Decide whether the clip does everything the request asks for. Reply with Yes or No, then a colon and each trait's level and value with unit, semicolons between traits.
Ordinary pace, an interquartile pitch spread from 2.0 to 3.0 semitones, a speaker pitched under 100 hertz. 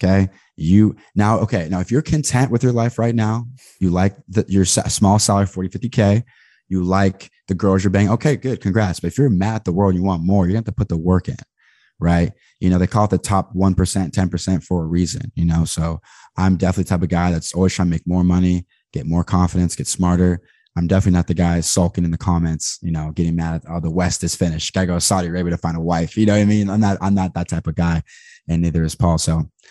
No: fast, 265 wpm; average, 2.7 semitones; very low, 90 Hz